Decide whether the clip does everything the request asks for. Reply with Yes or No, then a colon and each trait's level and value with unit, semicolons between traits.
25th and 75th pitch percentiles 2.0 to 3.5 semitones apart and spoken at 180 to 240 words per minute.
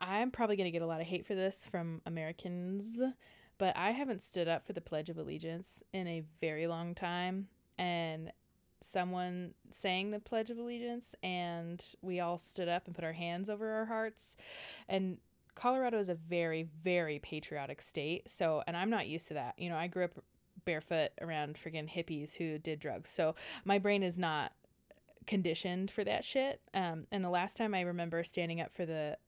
Yes: average, 3.2 semitones; average, 190 wpm